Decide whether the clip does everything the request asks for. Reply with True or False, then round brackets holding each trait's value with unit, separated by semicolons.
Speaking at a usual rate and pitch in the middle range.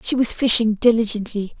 False (150 wpm; 225 Hz)